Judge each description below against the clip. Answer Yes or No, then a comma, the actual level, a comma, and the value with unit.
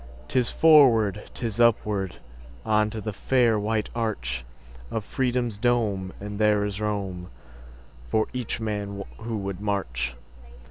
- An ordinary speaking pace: No, slow, 110 wpm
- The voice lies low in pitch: Yes, low, 105 Hz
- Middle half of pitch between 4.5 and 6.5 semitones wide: No, average, 4.0 semitones